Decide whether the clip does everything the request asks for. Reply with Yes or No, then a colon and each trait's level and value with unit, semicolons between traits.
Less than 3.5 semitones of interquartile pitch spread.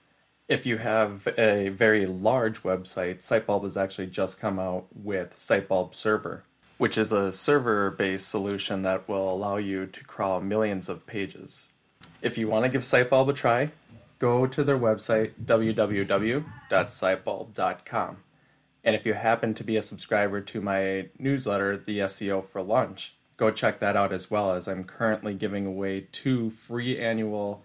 Yes: average, 2.7 semitones